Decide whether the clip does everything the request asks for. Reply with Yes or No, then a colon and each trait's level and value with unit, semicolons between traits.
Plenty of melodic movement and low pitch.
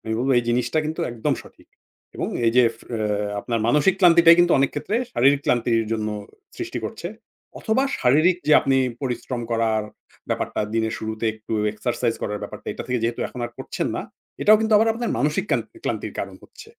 Yes: wide, 6.6 semitones; low, 125 Hz